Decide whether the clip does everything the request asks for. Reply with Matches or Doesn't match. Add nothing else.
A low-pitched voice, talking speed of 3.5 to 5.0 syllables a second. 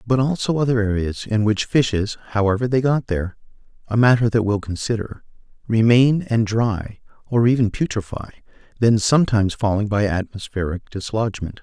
Doesn't match